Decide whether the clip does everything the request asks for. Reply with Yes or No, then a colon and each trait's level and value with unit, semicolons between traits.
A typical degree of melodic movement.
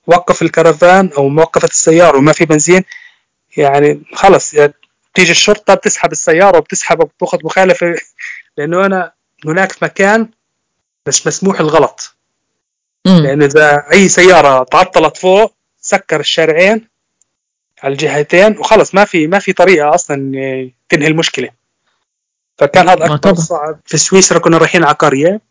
Yes: average, 3.5 semitones